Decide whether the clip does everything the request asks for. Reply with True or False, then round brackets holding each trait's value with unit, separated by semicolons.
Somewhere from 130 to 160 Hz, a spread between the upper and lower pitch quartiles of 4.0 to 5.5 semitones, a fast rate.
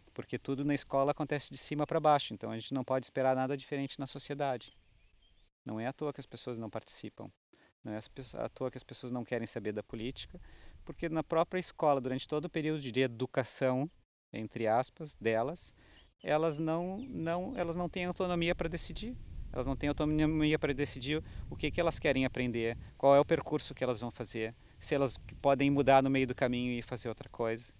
True (135 Hz; 4.3 semitones; 205 wpm)